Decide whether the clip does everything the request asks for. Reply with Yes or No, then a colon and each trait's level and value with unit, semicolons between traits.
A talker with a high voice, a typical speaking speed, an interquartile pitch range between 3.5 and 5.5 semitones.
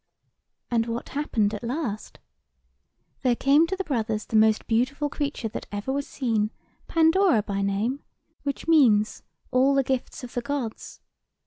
Yes: high, 245 Hz; average, 155 wpm; average, 4.6 semitones